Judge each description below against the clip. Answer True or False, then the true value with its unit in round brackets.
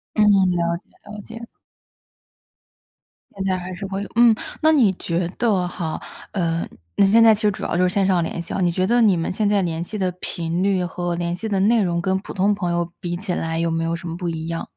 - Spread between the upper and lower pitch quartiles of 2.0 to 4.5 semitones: True (3.0 semitones)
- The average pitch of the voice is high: False (180 Hz)